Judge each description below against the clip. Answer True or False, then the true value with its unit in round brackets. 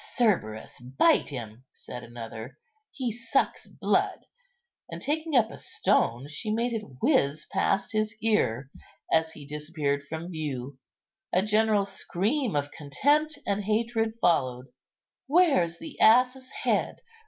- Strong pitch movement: True (8.6 semitones)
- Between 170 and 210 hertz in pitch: True (185 Hz)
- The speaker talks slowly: True (130 wpm)